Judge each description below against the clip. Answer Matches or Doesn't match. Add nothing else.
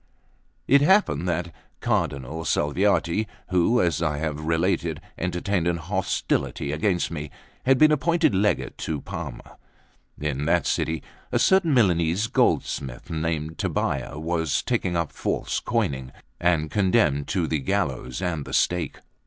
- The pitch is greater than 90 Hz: Doesn't match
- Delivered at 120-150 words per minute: Matches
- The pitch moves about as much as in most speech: Matches